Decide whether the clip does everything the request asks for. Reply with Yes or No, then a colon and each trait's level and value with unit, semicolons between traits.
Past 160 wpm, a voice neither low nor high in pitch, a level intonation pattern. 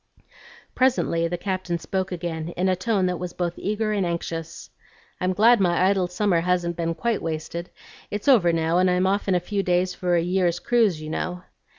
Yes: average, 200 wpm; medium, 180 Hz; narrow, 2.2 semitones